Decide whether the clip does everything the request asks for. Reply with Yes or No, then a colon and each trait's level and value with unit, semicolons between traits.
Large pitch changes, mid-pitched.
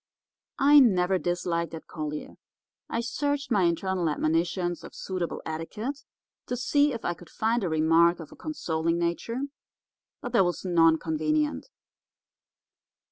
Yes: wide, 5.9 semitones; medium, 175 Hz